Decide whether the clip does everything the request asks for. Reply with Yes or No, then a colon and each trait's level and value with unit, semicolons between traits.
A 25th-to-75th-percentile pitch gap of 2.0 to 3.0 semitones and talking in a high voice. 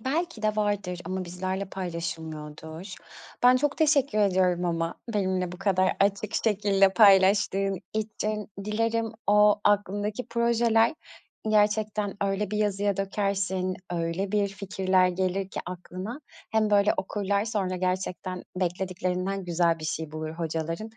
Yes: narrow, 2.5 semitones; high, 195 Hz